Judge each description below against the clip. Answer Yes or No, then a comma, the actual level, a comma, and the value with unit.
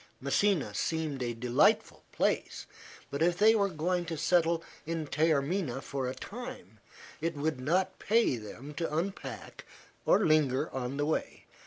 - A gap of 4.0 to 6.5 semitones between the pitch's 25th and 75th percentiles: Yes, average, 4.9 semitones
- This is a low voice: No, medium, 155 Hz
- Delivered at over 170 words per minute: No, average, 150 wpm